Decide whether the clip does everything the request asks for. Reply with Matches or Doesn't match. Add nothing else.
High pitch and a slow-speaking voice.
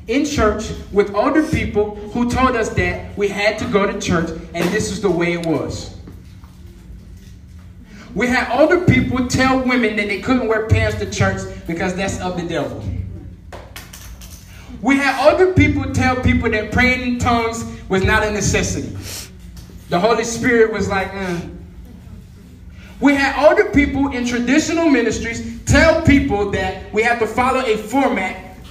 Doesn't match